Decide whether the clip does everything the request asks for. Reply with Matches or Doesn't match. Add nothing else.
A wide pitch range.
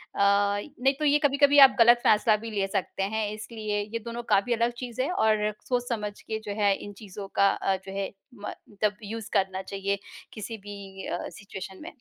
Doesn't match